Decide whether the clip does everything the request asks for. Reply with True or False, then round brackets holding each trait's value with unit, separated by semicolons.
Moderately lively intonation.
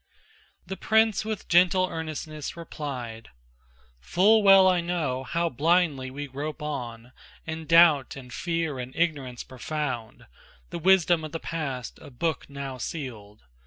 True (4.7 semitones)